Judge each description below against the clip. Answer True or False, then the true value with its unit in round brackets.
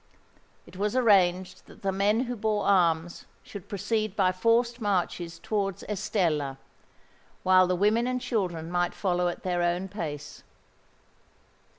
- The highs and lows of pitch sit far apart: False (3.2 semitones)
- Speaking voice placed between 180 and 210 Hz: True (190 Hz)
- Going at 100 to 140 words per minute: True (135 wpm)